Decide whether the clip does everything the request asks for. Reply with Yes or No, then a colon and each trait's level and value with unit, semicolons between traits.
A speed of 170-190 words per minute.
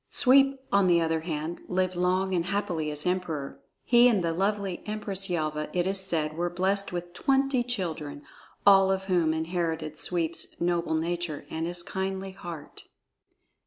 No: average, 160 wpm